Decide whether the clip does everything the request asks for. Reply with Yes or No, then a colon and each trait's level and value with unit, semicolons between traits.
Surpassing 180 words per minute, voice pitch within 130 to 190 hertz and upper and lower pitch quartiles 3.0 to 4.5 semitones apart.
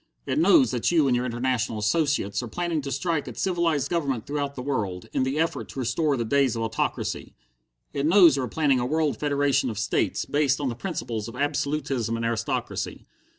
Yes: average, 200 wpm; medium, 140 Hz; average, 4.2 semitones